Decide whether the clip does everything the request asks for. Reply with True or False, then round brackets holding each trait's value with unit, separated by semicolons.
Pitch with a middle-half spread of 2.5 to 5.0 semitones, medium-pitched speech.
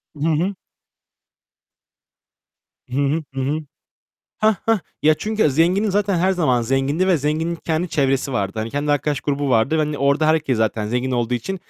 True (4.3 semitones; 150 Hz)